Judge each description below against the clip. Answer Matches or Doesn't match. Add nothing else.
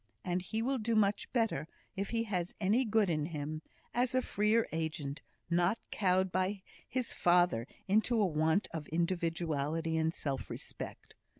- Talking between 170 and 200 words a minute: Doesn't match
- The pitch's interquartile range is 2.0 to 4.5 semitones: Doesn't match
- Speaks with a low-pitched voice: Doesn't match